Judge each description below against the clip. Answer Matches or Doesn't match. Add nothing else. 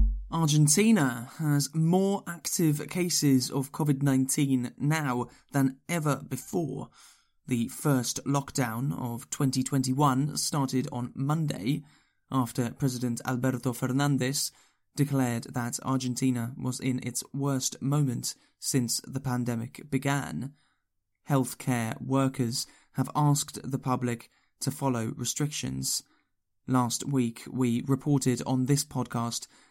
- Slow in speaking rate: Matches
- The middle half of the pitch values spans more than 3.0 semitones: Doesn't match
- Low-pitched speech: Matches